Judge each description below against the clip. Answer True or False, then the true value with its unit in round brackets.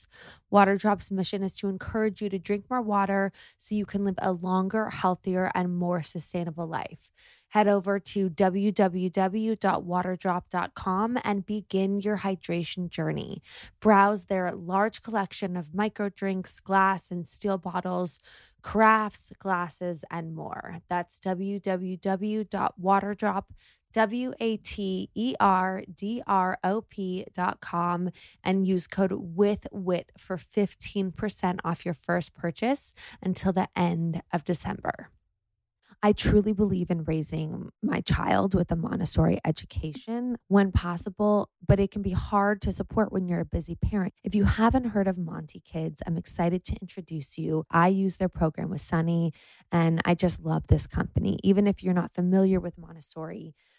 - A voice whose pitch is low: False (190 Hz)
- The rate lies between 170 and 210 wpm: False (145 wpm)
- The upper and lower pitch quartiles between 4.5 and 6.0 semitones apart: False (2.5 semitones)